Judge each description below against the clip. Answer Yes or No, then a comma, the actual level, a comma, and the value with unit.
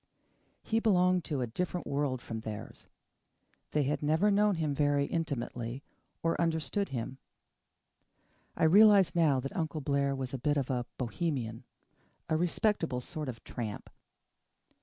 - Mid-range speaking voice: Yes, medium, 145 Hz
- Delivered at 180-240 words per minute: No, average, 140 wpm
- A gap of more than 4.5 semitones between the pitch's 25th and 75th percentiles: Yes, average, 4.9 semitones